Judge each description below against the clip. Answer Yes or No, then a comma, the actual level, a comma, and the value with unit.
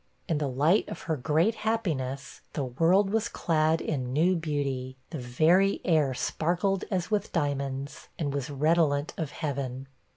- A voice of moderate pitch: Yes, medium, 155 Hz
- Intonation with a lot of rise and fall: No, average, 4.0 semitones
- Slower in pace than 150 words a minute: No, average, 155 wpm